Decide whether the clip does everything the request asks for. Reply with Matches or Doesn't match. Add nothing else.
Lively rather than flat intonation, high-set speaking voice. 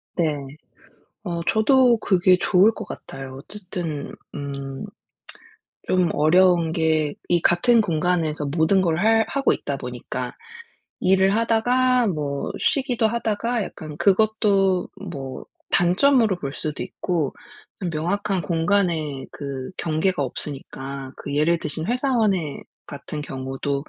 Doesn't match